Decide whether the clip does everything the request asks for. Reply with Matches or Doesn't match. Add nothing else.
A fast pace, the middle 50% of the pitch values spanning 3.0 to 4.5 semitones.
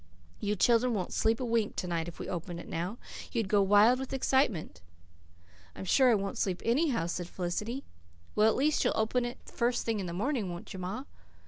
Doesn't match